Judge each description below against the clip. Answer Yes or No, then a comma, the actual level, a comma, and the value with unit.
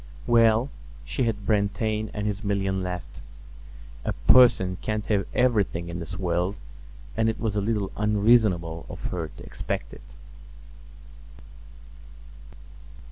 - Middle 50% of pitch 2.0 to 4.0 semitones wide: Yes, average, 3.3 semitones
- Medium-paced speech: No, slow, 125 wpm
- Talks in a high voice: No, low, 105 Hz